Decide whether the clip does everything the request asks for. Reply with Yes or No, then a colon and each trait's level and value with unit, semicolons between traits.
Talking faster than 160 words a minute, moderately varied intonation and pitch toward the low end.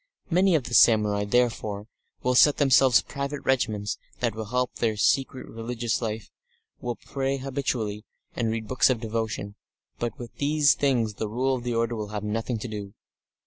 Yes: average, 175 wpm; average, 3.3 semitones; low, 120 Hz